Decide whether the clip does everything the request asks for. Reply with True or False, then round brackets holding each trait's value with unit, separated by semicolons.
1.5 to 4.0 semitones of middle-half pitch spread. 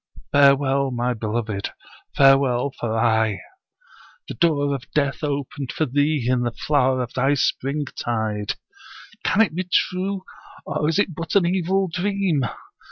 False (4.7 semitones)